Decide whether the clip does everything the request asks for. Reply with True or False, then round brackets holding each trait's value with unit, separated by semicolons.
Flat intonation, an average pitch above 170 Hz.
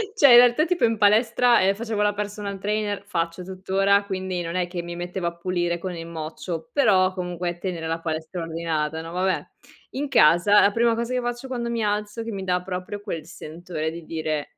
False (3.7 semitones; 185 Hz)